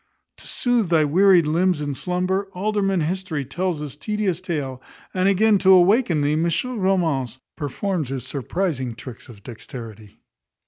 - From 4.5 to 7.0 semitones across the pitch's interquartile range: Yes, wide, 5.4 semitones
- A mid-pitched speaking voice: Yes, medium, 170 Hz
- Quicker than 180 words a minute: No, average, 145 wpm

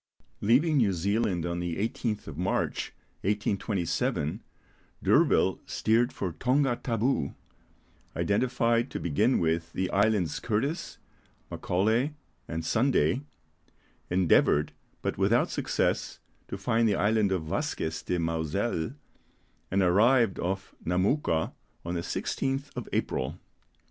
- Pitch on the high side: No, low, 100 Hz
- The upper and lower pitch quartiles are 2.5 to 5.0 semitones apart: No, wide, 5.4 semitones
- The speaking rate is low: Yes, slow, 115 wpm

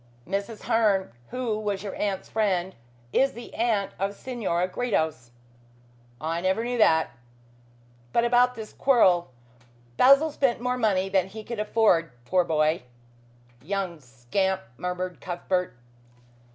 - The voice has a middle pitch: No, high, 195 Hz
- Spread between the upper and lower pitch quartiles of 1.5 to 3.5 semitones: No, average, 4.8 semitones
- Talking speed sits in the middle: No, slow, 130 wpm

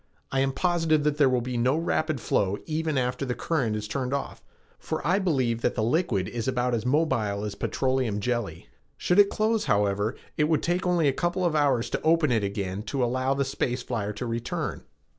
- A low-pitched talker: Yes, low, 130 Hz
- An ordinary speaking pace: No, fast, 210 wpm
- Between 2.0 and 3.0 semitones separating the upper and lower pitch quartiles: No, average, 5.3 semitones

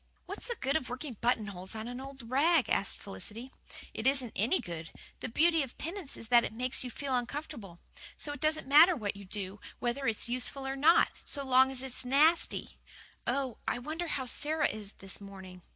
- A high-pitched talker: Yes, very high, 255 Hz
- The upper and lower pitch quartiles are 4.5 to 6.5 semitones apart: Yes, average, 4.8 semitones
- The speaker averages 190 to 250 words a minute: Yes, average, 200 wpm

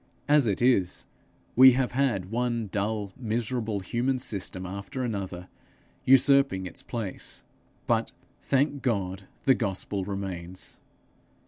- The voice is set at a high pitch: No, low, 110 Hz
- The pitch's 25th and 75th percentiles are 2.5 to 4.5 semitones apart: No, average, 5.0 semitones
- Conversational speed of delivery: No, slow, 115 wpm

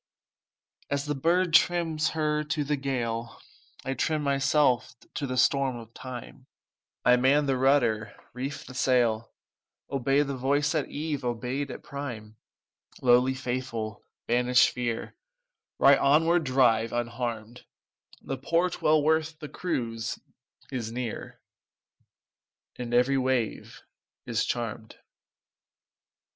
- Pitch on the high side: No, low, 130 Hz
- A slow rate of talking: Yes, slow, 120 wpm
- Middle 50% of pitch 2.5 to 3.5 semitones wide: Yes, average, 3.2 semitones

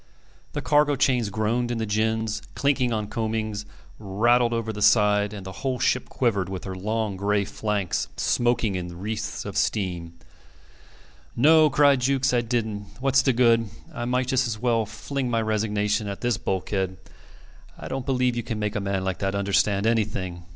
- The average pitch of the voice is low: Yes, low, 110 Hz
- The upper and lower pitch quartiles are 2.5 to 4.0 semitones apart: Yes, average, 3.2 semitones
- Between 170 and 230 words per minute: Yes, average, 175 wpm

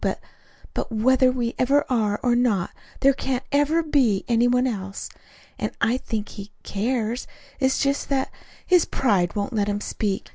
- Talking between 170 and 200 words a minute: Yes, average, 175 wpm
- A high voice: Yes, high, 245 Hz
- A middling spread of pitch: Yes, average, 4.1 semitones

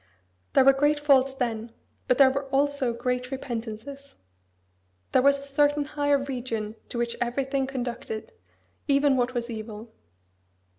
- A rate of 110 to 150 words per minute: Yes, average, 140 wpm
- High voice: Yes, very high, 265 Hz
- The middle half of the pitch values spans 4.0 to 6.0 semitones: No, average, 2.7 semitones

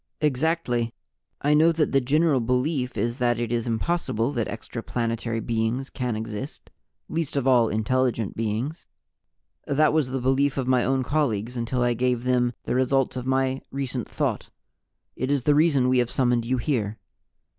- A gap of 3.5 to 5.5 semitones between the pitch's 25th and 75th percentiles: No, average, 2.8 semitones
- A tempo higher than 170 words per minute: No, average, 165 wpm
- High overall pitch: No, low, 125 Hz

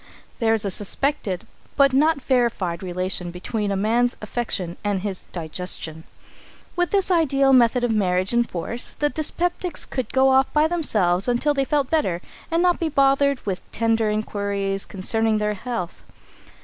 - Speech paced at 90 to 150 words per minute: No, average, 160 wpm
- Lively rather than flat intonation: Yes, wide, 6.0 semitones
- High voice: Yes, high, 230 Hz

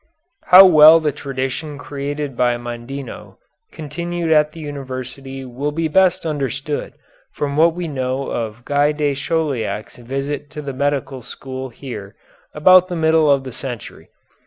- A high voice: No, medium, 140 Hz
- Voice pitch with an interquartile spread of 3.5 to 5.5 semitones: No, average, 3.0 semitones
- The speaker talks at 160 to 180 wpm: No, average, 145 wpm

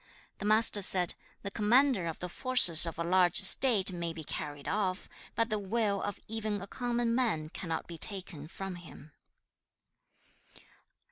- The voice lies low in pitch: No, high, 195 Hz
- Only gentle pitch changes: No, average, 4.5 semitones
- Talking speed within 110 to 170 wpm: Yes, average, 155 wpm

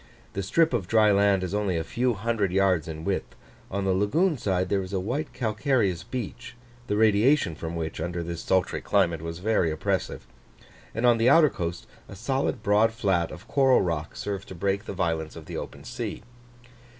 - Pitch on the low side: Yes, low, 100 Hz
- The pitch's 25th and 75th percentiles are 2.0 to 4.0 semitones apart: No, average, 4.6 semitones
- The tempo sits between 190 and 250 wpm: Yes, average, 195 wpm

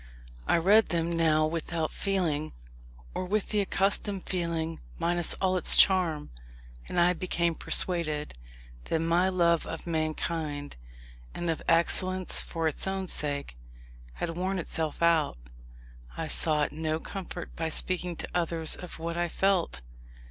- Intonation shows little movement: Yes, narrow, 2.3 semitones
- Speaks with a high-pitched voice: No, medium, 170 Hz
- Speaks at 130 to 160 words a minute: Yes, average, 140 wpm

